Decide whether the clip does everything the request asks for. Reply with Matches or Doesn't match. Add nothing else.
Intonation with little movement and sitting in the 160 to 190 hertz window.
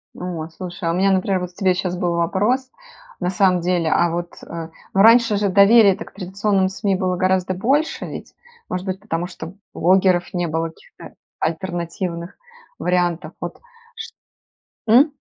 Matches